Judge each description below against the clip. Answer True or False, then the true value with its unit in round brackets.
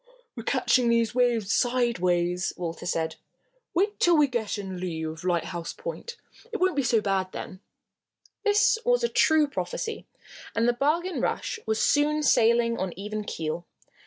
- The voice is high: True (235 Hz)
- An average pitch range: False (8.7 semitones)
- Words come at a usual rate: True (160 wpm)